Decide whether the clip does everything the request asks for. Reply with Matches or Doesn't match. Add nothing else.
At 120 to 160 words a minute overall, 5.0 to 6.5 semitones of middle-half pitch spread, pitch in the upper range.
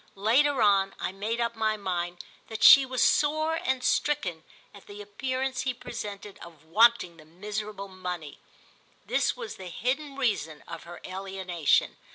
Matches